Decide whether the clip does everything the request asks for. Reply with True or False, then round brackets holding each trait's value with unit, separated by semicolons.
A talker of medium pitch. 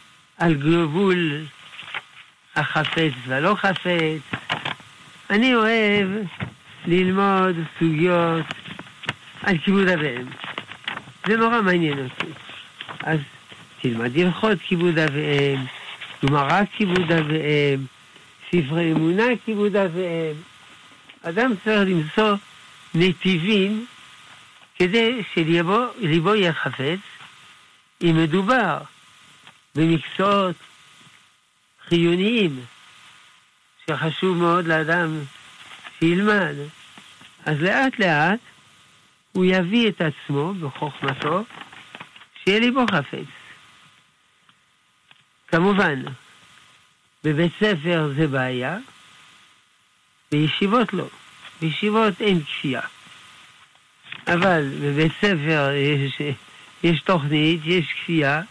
True (165 Hz)